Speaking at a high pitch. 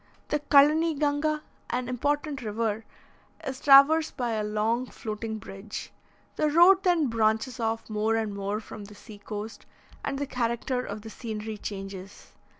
Yes: high, 230 Hz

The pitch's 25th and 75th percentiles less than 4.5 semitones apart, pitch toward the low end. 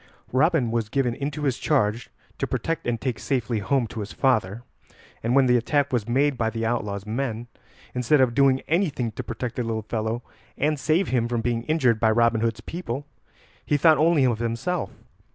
Yes: average, 3.6 semitones; low, 120 Hz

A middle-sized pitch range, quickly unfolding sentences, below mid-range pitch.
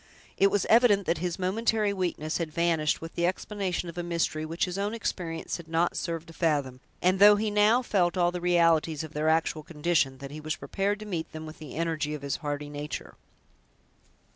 No: average, 3.4 semitones; fast, 210 wpm; medium, 170 Hz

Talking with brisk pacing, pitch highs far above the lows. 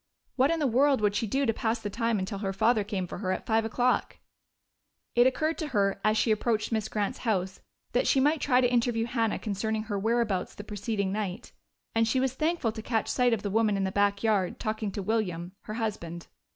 No: fast, 225 wpm; average, 3.0 semitones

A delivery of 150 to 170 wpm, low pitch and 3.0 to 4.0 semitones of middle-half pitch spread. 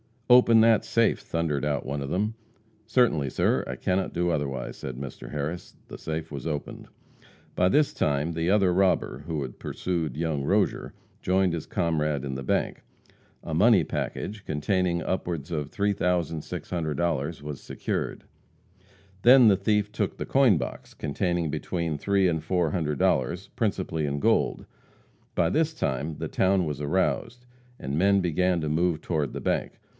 No: average, 160 wpm; very low, 85 Hz; average, 4.5 semitones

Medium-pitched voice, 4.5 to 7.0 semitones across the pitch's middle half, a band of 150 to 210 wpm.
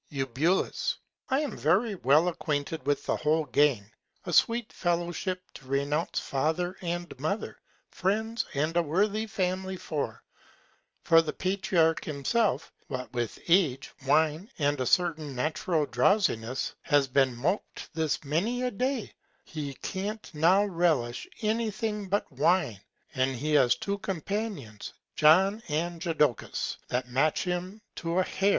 No: medium, 165 Hz; average, 5.2 semitones; average, 140 wpm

